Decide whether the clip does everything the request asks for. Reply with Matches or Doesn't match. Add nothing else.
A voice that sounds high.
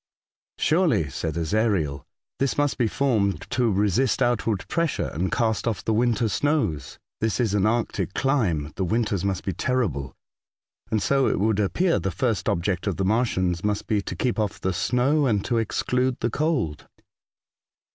Doesn't match